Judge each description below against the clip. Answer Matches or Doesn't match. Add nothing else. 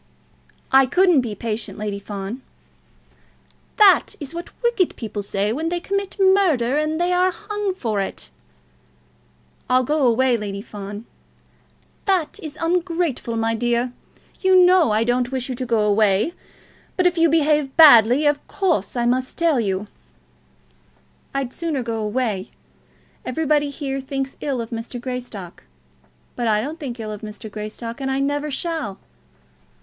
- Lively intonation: Matches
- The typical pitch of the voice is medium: Doesn't match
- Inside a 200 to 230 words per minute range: Doesn't match